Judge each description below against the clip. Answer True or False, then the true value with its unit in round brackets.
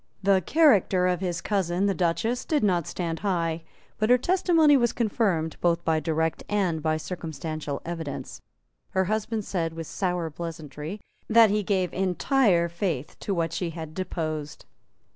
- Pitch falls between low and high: True (180 Hz)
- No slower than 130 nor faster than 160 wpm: True (155 wpm)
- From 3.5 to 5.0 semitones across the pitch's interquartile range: True (4.0 semitones)